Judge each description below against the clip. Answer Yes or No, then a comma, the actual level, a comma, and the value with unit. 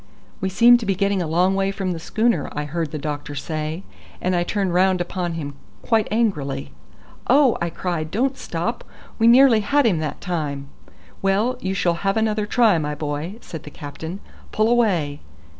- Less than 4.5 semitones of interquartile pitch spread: No, wide, 5.4 semitones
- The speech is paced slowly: No, average, 185 wpm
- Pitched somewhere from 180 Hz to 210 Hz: Yes, medium, 185 Hz